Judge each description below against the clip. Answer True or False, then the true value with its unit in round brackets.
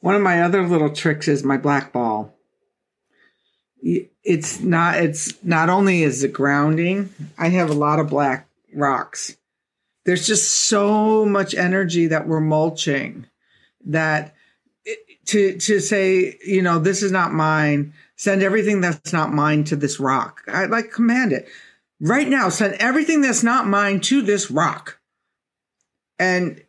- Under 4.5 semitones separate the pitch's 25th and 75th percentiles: False (4.8 semitones)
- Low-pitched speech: False (180 Hz)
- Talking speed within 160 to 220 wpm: False (150 wpm)